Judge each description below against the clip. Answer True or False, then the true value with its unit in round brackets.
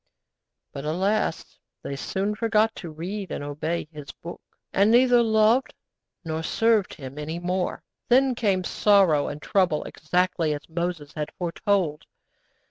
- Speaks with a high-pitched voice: False (180 Hz)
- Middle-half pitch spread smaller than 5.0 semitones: False (5.4 semitones)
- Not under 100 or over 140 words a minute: True (135 wpm)